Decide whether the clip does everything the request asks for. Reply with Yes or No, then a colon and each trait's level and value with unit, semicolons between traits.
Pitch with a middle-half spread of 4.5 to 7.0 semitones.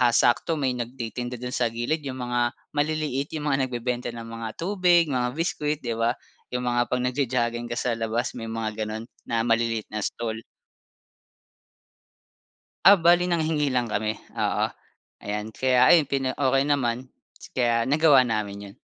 No: average, 3.5 semitones